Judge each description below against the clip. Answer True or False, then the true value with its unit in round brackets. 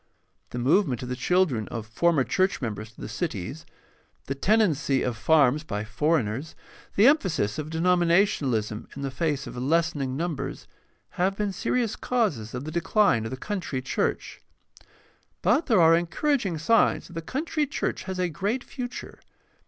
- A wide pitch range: True (7.0 semitones)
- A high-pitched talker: False (160 Hz)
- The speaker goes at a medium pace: True (160 wpm)